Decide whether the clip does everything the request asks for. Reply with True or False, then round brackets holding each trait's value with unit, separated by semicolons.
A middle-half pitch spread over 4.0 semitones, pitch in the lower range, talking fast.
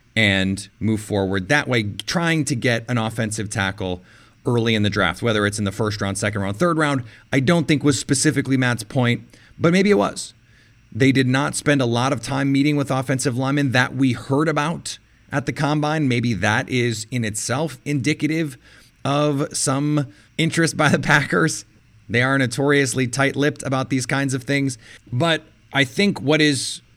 False (4.4 semitones; 130 Hz; 180 wpm)